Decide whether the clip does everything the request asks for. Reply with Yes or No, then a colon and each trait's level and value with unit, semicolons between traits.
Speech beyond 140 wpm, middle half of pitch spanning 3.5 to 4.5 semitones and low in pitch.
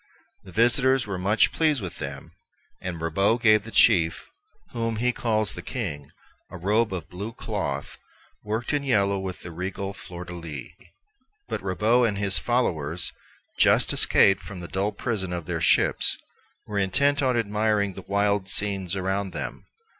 Yes: average, 160 wpm; average, 3.8 semitones; low, 100 Hz